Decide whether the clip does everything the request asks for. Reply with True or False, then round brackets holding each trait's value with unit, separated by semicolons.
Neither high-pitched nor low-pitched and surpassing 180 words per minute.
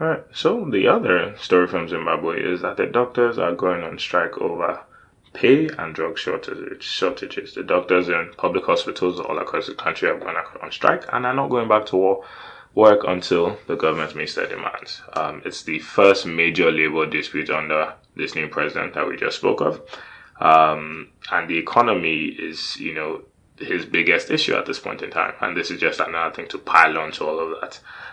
False (120 Hz; 190 wpm)